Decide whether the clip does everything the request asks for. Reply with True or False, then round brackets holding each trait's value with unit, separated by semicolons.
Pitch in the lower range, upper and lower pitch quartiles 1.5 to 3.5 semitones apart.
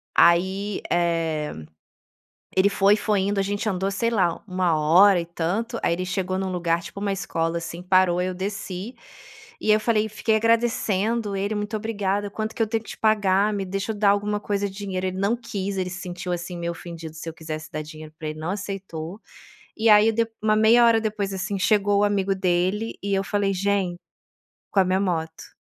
False (195 Hz; 2.7 semitones)